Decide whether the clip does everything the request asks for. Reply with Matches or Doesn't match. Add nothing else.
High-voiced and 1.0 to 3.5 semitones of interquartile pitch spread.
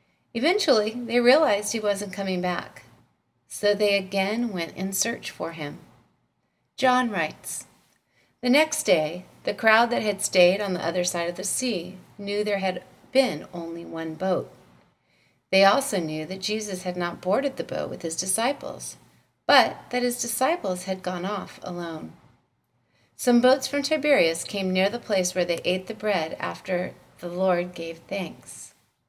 Doesn't match